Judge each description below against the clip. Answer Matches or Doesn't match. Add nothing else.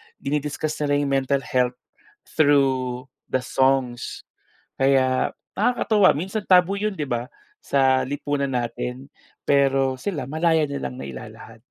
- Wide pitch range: Doesn't match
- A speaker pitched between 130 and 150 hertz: Matches